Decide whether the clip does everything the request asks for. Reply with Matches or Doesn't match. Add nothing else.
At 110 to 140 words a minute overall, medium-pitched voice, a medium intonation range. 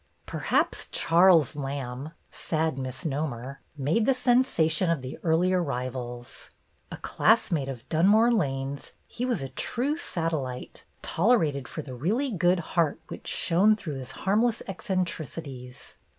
Doesn't match